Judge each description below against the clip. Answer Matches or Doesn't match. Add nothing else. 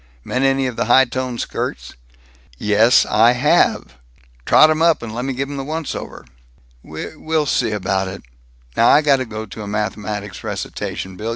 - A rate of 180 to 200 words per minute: Matches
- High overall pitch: Doesn't match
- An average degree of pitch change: Matches